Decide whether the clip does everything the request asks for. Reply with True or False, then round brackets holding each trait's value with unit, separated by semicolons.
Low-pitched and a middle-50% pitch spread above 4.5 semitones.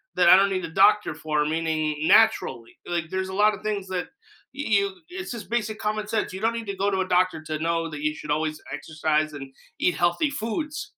False (185 Hz; 5.2 semitones)